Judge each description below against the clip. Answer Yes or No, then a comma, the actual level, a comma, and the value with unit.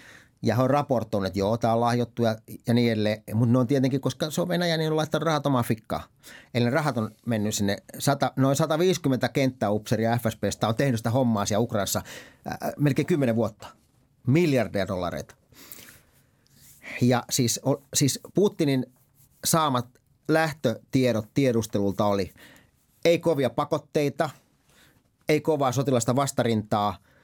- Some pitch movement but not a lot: Yes, average, 4.0 semitones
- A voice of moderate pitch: No, low, 130 Hz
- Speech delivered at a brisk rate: No, average, 145 wpm